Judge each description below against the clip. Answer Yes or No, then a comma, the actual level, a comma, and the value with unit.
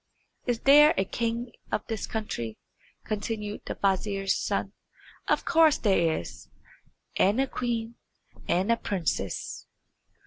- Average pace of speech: No, slow, 125 wpm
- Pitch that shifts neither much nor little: Yes, average, 3.4 semitones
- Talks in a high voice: Yes, high, 215 Hz